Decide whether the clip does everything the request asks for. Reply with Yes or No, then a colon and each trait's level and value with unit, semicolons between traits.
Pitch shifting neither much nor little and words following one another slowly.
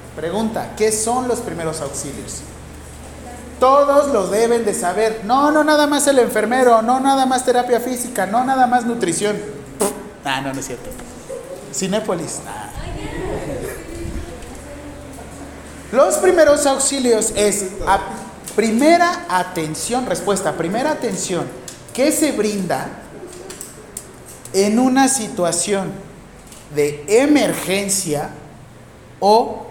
No: wide, 6.3 semitones; slow, 105 wpm